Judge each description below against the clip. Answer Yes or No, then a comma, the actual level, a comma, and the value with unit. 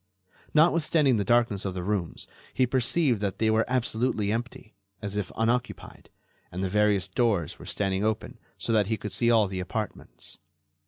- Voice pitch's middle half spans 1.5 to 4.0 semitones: Yes, average, 3.4 semitones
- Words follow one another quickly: No, average, 170 wpm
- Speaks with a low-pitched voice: Yes, low, 110 Hz